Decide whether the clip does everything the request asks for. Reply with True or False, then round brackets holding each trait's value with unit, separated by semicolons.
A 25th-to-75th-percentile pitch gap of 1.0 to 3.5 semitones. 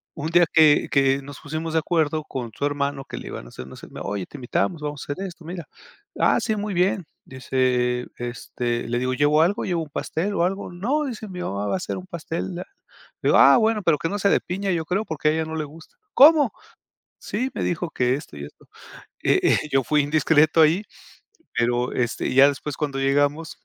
False (4.7 semitones)